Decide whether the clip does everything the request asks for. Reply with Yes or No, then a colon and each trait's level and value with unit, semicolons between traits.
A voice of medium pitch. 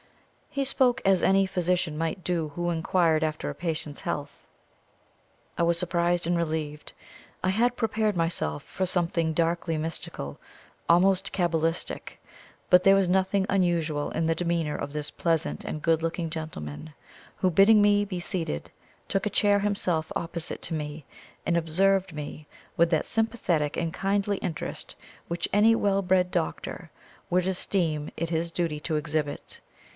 Yes: medium, 170 Hz